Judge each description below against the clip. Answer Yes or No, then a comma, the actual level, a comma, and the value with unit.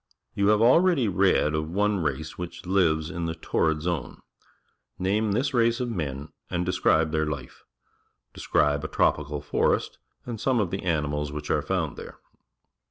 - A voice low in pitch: Yes, very low, 85 Hz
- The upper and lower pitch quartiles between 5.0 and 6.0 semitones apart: Yes, average, 5.3 semitones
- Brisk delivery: No, average, 165 wpm